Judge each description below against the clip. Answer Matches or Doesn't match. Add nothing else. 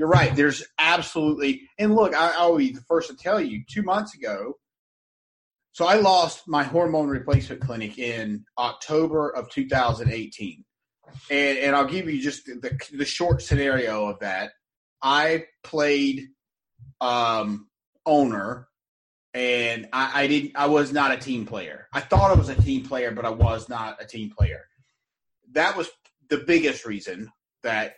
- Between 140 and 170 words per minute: Matches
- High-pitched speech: Doesn't match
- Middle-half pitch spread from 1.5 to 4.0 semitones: Doesn't match